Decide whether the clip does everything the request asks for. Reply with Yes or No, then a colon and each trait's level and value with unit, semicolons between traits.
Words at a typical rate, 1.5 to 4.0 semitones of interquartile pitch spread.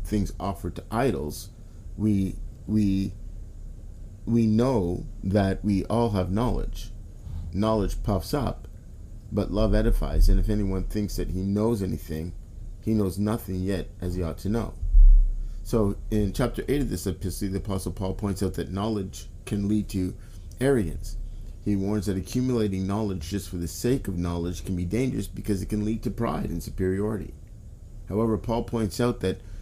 Yes: average, 165 wpm; average, 2.9 semitones